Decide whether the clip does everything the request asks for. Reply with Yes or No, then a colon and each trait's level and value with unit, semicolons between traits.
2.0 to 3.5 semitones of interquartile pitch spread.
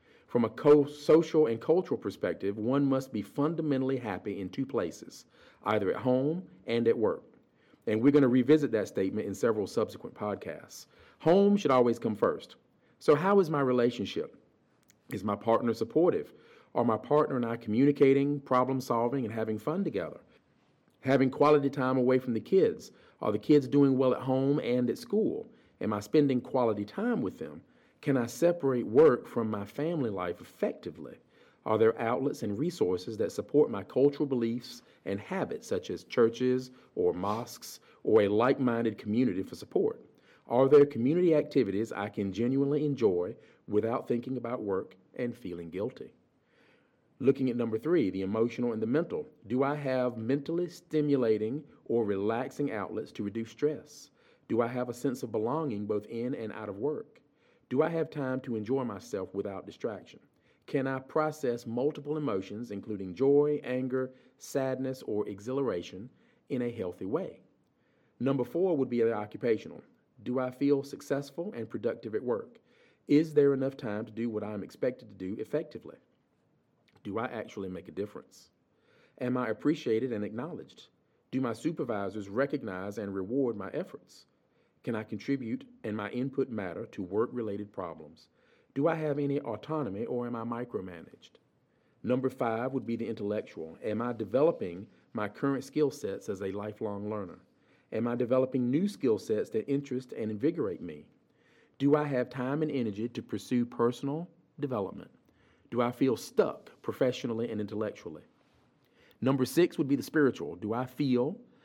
No: average, 4.1 semitones